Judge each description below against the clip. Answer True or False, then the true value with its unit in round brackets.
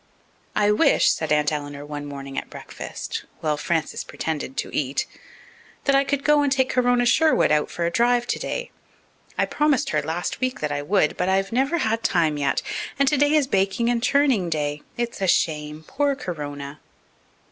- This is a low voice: False (190 Hz)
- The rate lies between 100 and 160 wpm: False (180 wpm)